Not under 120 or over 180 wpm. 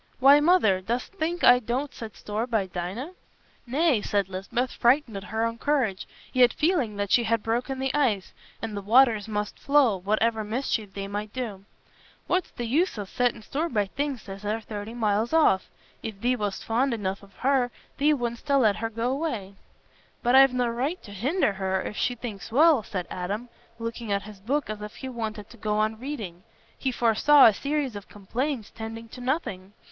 No: average, 195 wpm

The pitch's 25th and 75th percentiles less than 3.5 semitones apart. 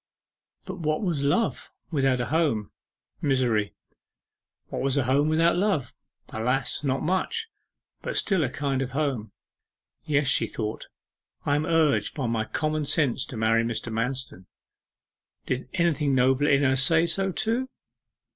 No: average, 4.2 semitones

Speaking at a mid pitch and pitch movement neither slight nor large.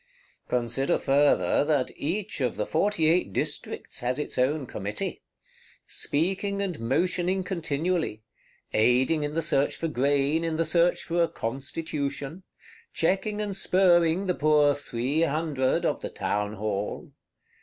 Yes: medium, 150 Hz; average, 4.7 semitones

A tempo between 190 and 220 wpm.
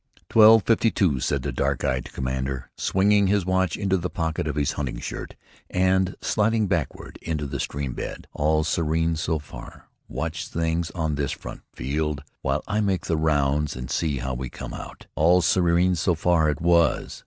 No: average, 180 wpm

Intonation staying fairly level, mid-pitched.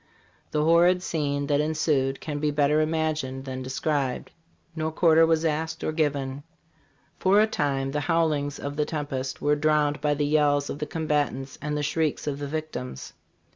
Yes: narrow, 1.8 semitones; medium, 150 Hz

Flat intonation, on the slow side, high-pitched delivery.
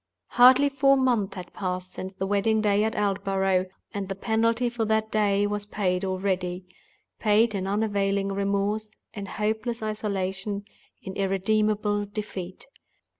Yes: narrow, 2.1 semitones; slow, 130 wpm; high, 205 Hz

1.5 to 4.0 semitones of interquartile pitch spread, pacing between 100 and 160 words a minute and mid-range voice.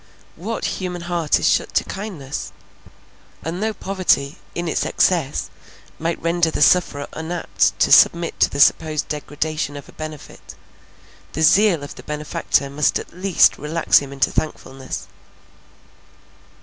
Yes: average, 3.2 semitones; average, 140 wpm; medium, 160 Hz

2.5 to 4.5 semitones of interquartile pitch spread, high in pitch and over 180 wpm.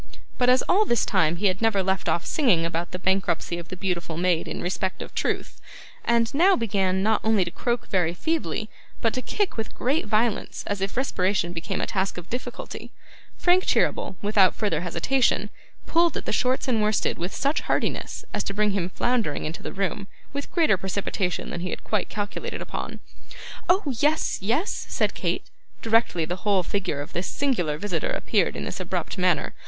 No: average, 5.1 semitones; high, 200 Hz; average, 190 wpm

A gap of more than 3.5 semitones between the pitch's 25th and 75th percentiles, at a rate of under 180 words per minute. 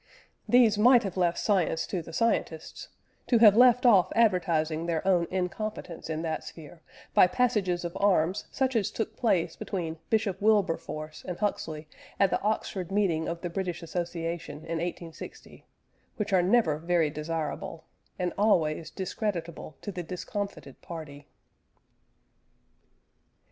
Yes: average, 4.1 semitones; average, 140 wpm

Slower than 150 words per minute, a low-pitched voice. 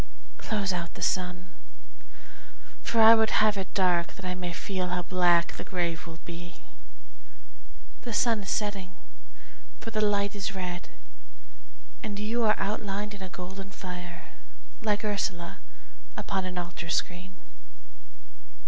No: average, 140 wpm; high, 190 Hz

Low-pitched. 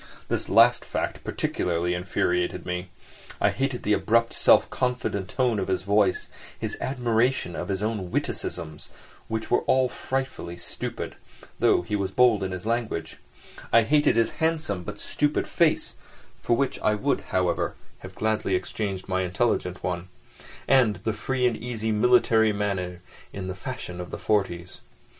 Yes: low, 105 Hz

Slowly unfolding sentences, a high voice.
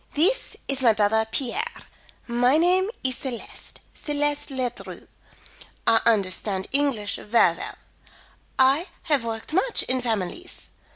Yes: slow, 120 wpm; very high, 260 Hz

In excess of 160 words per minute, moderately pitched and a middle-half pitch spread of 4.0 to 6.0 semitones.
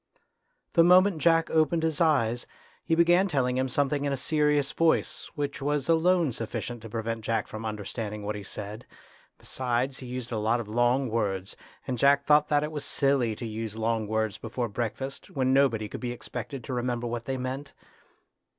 No: average, 185 wpm; low, 125 Hz; average, 4.4 semitones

